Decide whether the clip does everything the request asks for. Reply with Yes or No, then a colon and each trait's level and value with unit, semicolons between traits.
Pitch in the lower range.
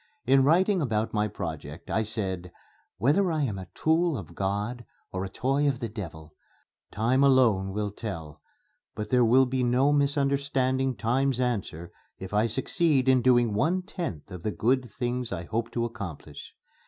Yes: low, 120 Hz